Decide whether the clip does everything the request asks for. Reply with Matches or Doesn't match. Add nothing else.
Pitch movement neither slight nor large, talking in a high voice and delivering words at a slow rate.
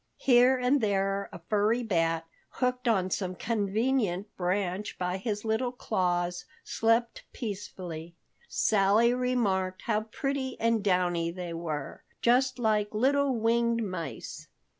Matches